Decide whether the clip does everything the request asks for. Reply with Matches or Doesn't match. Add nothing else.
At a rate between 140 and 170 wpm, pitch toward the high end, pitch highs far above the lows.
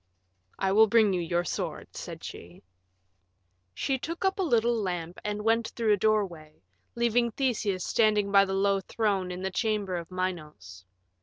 Doesn't match